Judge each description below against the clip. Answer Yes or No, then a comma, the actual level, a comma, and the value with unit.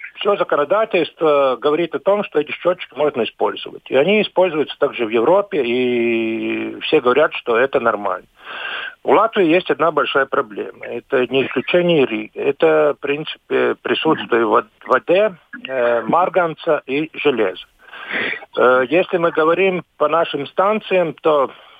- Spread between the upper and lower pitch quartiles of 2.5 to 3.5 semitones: No, average, 5.2 semitones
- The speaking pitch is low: No, medium, 155 Hz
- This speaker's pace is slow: No, average, 130 wpm